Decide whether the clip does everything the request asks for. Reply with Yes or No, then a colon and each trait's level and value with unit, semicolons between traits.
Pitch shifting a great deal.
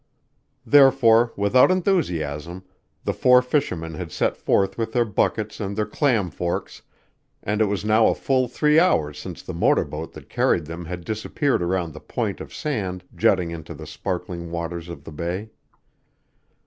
Yes: wide, 5.9 semitones